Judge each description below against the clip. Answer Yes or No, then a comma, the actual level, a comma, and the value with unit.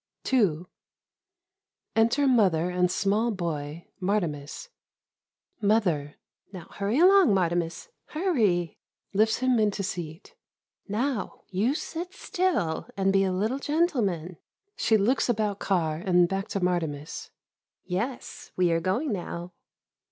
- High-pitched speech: Yes, high, 195 Hz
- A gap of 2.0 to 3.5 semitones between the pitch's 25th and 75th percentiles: No, average, 5.1 semitones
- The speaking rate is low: Yes, slow, 120 wpm